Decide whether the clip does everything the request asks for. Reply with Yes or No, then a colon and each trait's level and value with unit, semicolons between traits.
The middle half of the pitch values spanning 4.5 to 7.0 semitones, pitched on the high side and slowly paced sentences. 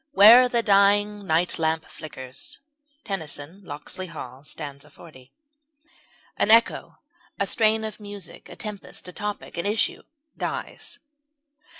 Yes: average, 5.0 semitones; high, 195 Hz; slow, 120 wpm